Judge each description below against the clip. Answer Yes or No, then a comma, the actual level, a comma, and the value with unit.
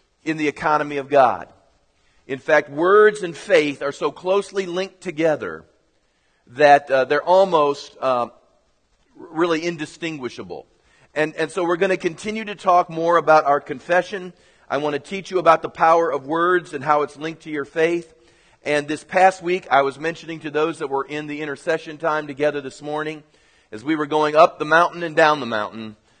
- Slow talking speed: No, average, 185 wpm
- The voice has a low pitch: No, medium, 155 Hz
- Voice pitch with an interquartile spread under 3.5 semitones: Yes, average, 2.8 semitones